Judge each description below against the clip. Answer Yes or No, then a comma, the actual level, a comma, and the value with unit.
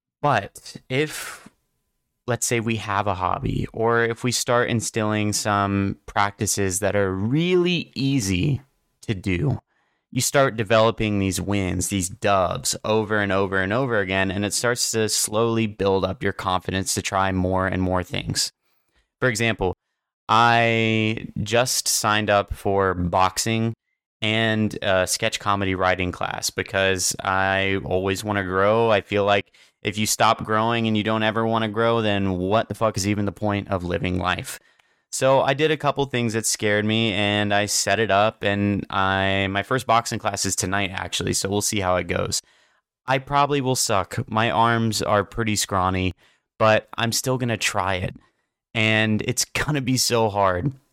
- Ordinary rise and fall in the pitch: Yes, average, 3.1 semitones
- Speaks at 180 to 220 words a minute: No, average, 170 wpm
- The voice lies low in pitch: Yes, low, 105 Hz